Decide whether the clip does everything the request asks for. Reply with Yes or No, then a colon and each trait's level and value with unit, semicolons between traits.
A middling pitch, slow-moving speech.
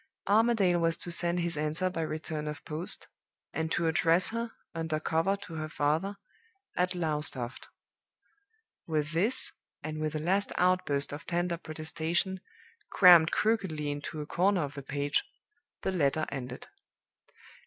No: medium, 165 Hz; average, 145 wpm